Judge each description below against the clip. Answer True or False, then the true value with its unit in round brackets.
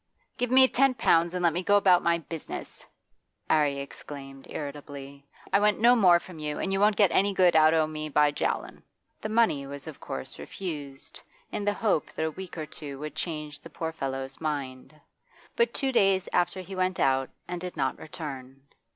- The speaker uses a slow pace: False (195 wpm)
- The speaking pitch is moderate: True (160 Hz)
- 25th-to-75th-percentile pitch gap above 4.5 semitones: True (5.0 semitones)